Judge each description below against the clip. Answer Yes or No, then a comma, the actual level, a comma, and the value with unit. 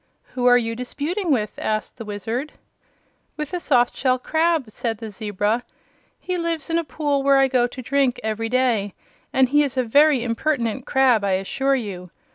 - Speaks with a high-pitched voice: Yes, very high, 255 Hz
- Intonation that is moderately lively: Yes, average, 4.0 semitones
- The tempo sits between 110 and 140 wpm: No, average, 185 wpm